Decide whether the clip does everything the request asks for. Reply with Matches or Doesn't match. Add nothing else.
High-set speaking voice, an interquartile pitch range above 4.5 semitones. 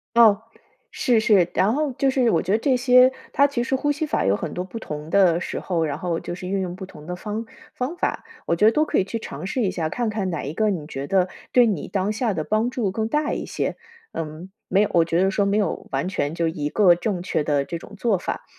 Matches